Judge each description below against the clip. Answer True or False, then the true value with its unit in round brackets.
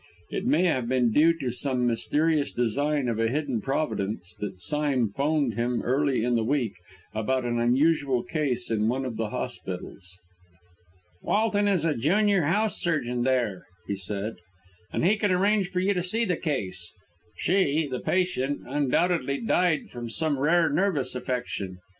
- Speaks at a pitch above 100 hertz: True (135 Hz)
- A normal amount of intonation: False (5.9 semitones)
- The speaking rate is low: False (160 wpm)